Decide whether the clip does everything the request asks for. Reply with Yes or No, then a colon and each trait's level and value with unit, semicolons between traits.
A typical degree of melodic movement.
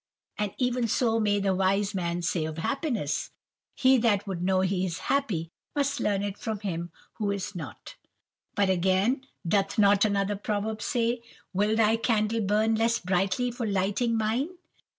Yes: average, 3.1 semitones